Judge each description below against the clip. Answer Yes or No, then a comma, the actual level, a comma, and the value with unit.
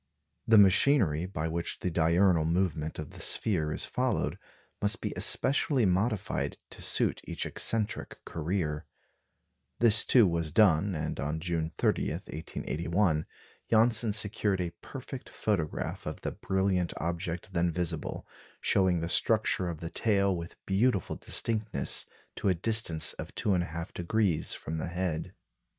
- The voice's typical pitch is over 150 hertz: No, very low, 90 Hz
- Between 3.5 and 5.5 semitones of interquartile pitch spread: Yes, average, 4.2 semitones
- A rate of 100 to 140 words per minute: Yes, slow, 135 wpm